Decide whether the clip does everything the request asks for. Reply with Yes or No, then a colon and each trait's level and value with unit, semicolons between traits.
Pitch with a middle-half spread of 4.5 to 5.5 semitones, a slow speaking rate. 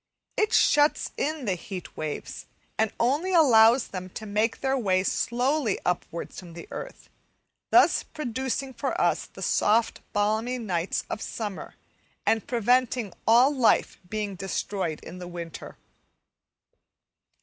Yes: average, 5.2 semitones; slow, 130 wpm